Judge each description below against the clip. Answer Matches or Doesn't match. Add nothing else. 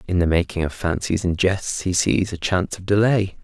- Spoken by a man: Matches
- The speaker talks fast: Matches